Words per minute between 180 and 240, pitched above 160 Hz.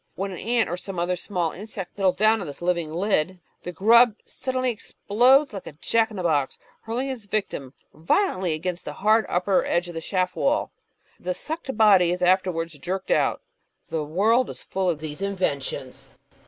Yes: average, 185 wpm; medium, 185 Hz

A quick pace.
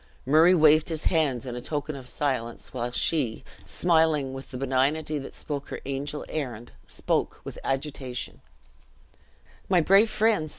No: average, 140 wpm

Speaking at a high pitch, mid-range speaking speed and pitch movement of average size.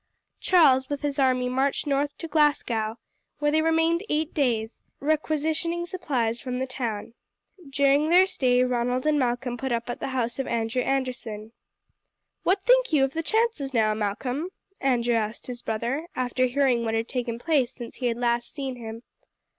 Yes: very high, 260 Hz; average, 170 wpm; average, 3.9 semitones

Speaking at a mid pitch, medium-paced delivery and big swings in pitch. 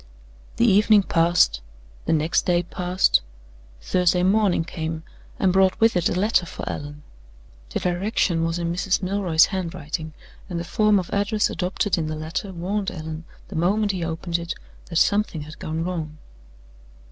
No: medium, 175 Hz; average, 160 wpm; average, 2.9 semitones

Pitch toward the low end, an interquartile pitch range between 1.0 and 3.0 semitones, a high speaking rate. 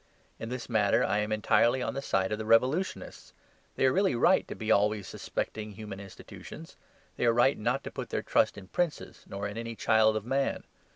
No: low, 110 Hz; average, 3.4 semitones; fast, 210 wpm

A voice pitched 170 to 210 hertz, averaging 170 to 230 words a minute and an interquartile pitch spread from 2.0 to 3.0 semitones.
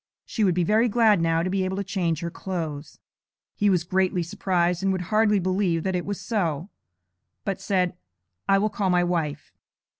Yes: medium, 185 Hz; average, 190 wpm; narrow, 2.6 semitones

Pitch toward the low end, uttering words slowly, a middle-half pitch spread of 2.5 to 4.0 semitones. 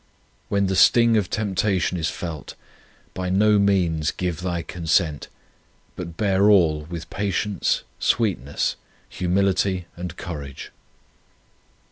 Yes: very low, 90 Hz; slow, 115 wpm; average, 3.2 semitones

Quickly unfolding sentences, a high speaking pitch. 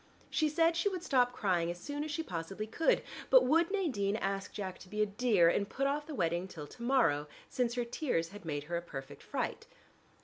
Yes: fast, 225 wpm; high, 215 Hz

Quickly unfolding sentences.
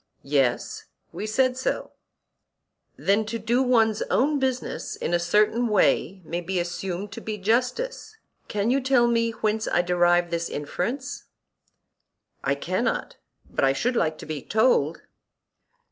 No: average, 145 wpm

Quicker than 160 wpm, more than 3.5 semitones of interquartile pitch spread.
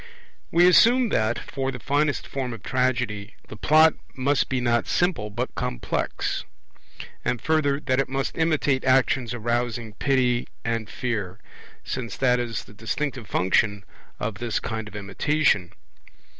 No: average, 145 wpm; average, 3.9 semitones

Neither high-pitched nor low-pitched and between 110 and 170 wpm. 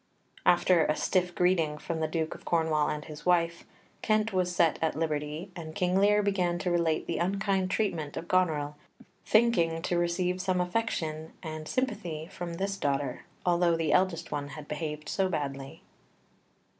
Yes: medium, 170 Hz; average, 165 wpm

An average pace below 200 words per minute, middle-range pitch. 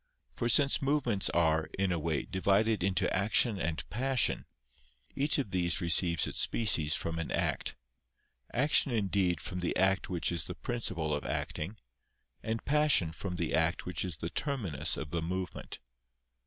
No: average, 160 wpm; very low, 95 Hz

